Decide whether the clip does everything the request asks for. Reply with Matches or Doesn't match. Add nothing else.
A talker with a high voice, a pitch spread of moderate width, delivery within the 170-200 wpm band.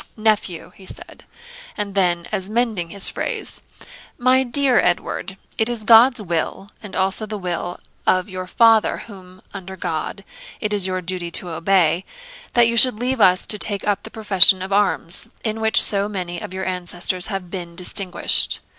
Matches